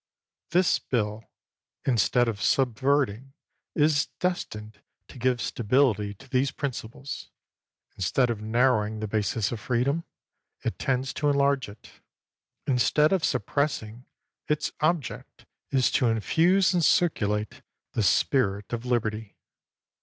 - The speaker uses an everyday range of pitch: Yes, average, 4.6 semitones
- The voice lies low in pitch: Yes, low, 125 Hz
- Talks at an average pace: No, slow, 120 wpm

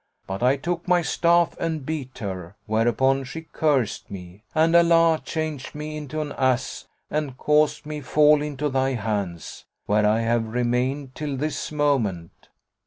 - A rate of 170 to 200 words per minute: No, average, 155 wpm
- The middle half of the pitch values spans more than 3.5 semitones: Yes, average, 4.8 semitones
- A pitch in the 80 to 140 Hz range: Yes, low, 135 Hz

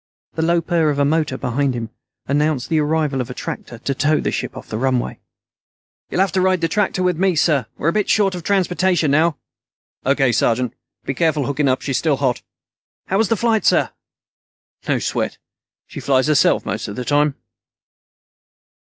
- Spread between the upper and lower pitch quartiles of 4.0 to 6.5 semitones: Yes, average, 4.5 semitones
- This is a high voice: No, medium, 150 Hz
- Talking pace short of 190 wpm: No, average, 195 wpm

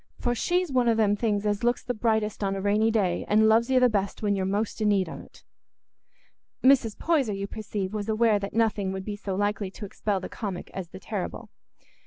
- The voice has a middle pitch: No, high, 210 Hz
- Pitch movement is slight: Yes, narrow, 2.3 semitones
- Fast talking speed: Yes, fast, 220 wpm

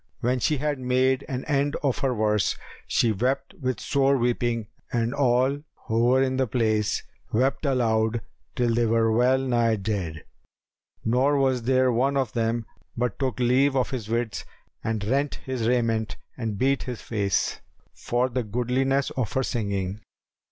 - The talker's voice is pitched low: Yes, low, 125 Hz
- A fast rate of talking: No, average, 160 wpm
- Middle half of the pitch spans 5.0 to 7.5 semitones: No, average, 2.8 semitones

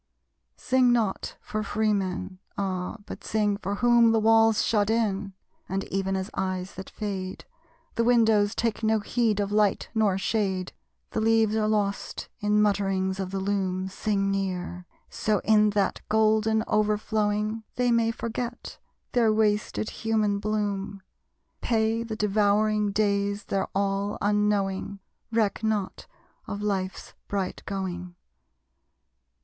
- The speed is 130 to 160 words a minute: Yes, slow, 135 wpm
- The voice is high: Yes, high, 210 Hz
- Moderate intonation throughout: No, narrow, 1.9 semitones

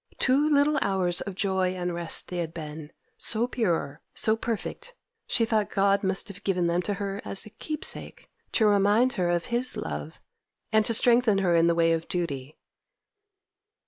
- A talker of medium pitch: No, high, 195 Hz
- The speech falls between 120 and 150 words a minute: No, average, 175 wpm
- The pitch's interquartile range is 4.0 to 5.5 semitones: Yes, average, 4.5 semitones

